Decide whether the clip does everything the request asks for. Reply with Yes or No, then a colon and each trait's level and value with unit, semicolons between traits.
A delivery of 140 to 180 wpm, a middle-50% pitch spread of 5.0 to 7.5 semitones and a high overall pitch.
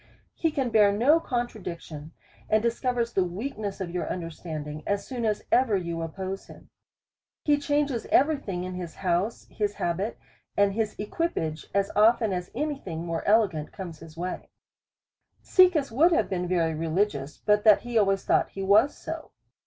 Yes: average, 170 wpm; wide, 5.4 semitones; high, 200 Hz